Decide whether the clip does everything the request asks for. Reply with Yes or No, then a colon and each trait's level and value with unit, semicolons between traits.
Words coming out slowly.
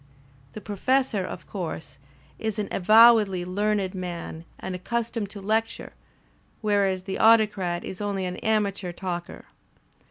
Yes: slow, 130 wpm